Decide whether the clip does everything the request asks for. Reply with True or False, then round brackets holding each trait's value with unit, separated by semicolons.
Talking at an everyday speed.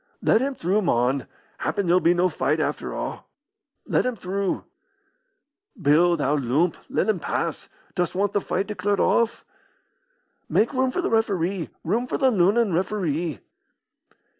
True (150 wpm)